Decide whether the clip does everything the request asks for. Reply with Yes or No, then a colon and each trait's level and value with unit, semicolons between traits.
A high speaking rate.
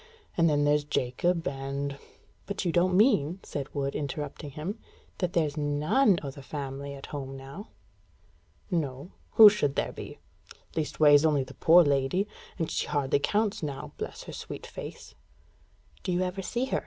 No: average, 170 wpm